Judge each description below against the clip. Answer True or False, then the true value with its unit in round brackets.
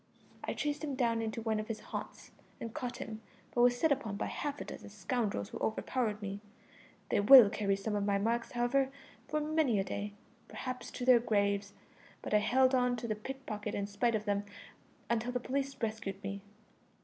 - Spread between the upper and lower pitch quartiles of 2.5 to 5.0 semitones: True (3.6 semitones)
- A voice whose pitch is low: False (225 Hz)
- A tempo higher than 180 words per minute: True (200 wpm)